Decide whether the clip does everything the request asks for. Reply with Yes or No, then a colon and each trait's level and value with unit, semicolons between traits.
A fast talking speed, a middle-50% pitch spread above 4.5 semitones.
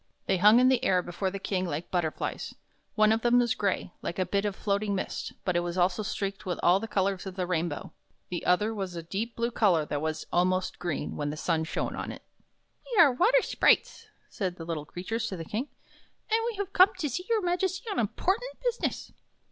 Yes: fast, 230 wpm; average, 5.2 semitones